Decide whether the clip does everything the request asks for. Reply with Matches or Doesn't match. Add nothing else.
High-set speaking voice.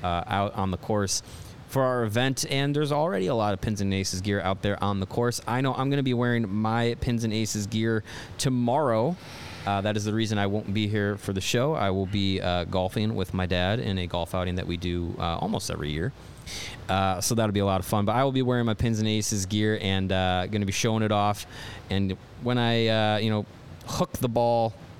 Doesn't match